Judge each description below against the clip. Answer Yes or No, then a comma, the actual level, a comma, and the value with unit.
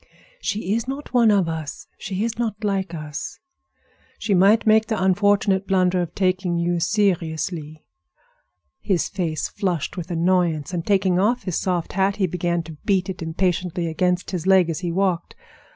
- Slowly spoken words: No, average, 170 wpm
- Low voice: No, medium, 185 Hz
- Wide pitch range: No, average, 2.7 semitones